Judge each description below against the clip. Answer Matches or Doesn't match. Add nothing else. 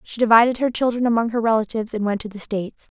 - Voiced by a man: Doesn't match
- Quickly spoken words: Matches